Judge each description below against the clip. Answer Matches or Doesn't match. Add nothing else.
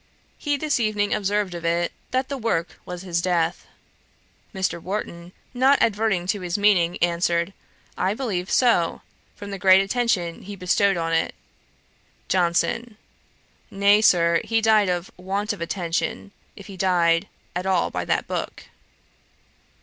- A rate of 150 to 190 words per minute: Doesn't match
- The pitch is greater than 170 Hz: Matches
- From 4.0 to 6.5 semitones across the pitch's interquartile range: Doesn't match